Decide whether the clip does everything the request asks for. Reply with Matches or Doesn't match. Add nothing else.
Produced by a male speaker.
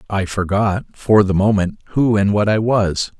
Matches